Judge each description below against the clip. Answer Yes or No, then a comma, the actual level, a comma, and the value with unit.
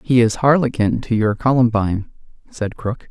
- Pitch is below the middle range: Yes, low, 115 Hz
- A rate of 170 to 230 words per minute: No, average, 155 wpm